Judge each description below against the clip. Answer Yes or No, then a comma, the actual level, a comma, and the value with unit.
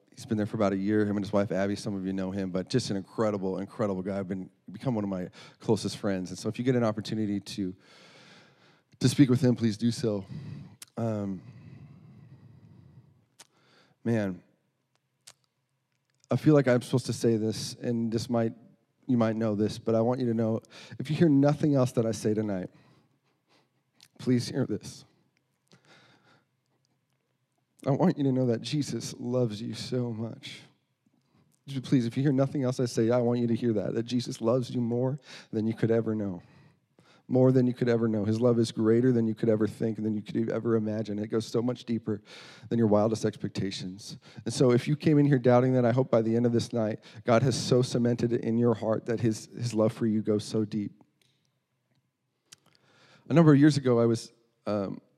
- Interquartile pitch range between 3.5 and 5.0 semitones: No, average, 3.0 semitones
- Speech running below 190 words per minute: No, fast, 205 wpm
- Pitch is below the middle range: Yes, low, 115 Hz